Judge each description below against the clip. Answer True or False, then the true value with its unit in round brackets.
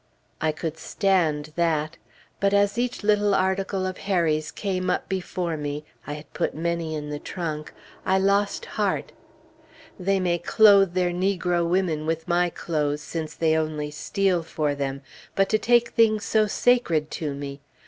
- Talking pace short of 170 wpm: True (160 wpm)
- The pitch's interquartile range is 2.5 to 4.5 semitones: True (4.0 semitones)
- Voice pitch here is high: False (175 Hz)